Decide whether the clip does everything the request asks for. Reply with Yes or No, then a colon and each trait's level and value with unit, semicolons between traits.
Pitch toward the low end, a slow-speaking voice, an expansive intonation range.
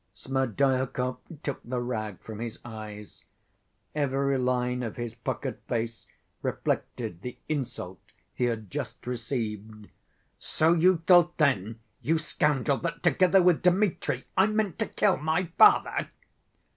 Yes: low, 130 Hz; slow, 130 wpm; wide, 5.8 semitones